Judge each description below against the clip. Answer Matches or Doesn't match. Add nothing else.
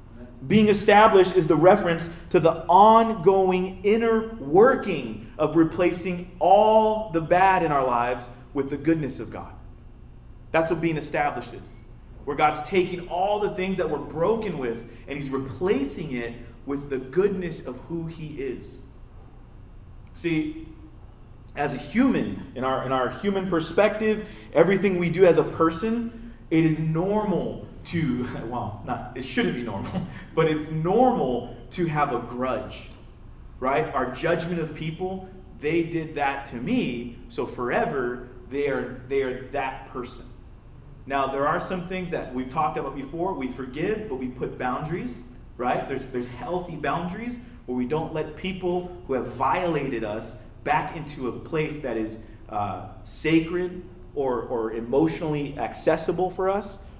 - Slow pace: Doesn't match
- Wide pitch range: Matches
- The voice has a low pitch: Doesn't match